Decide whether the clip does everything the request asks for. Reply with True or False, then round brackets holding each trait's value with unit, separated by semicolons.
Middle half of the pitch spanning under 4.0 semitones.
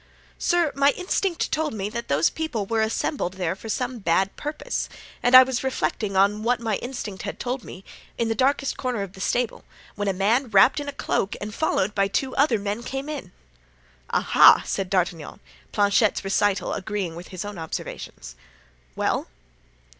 False (5.1 semitones)